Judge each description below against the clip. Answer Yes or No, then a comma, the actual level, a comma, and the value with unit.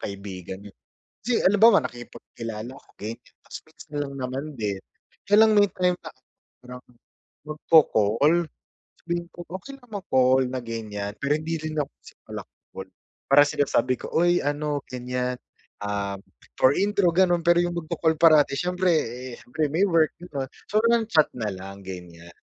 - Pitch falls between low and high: Yes, medium, 145 Hz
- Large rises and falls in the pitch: Yes, wide, 7.0 semitones